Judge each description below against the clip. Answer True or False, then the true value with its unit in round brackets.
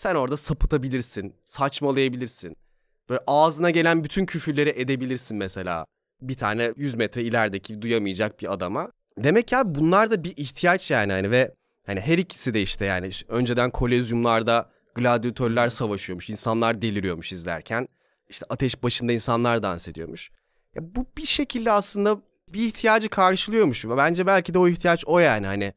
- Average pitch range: False (7.2 semitones)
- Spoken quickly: True (150 wpm)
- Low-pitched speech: True (125 Hz)